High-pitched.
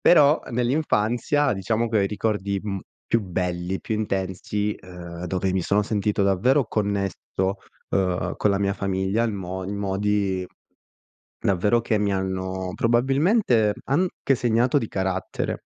No: low, 100 Hz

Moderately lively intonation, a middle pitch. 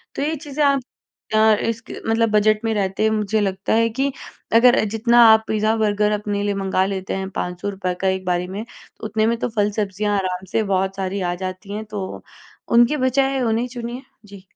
No: average, 3.0 semitones; high, 210 Hz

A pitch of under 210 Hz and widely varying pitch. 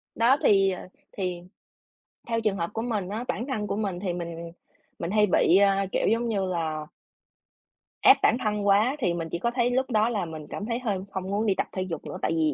No: high, 200 Hz; average, 4.2 semitones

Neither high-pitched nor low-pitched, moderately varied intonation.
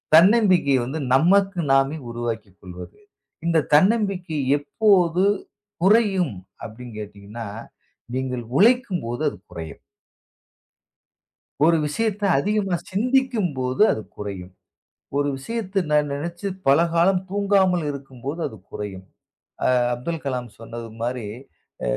No: medium, 155 Hz; wide, 8.1 semitones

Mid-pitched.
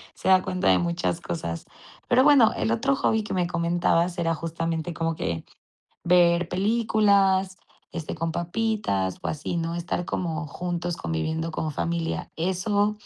Yes: medium, 170 Hz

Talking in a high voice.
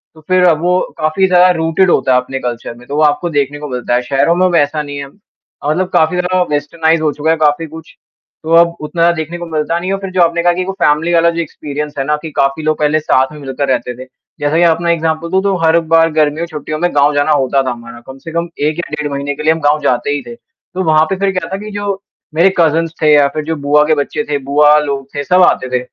No: medium, 155 Hz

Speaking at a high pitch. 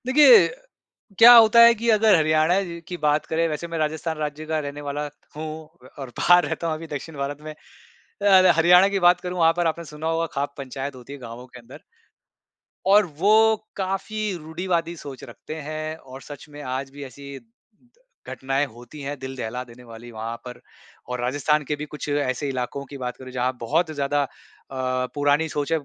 No: medium, 150 Hz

